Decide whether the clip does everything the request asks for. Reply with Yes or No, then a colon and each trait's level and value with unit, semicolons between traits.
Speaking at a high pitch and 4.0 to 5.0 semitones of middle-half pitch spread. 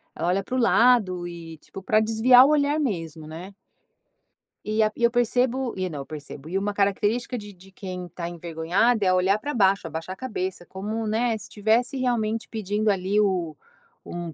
Yes: high, 200 Hz; average, 4.5 semitones